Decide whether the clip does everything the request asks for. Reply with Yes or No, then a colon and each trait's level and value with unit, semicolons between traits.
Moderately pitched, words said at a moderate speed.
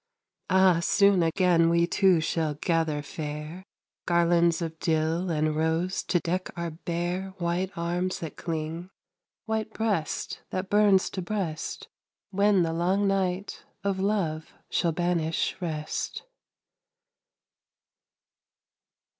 No: medium, 175 Hz; slow, 115 wpm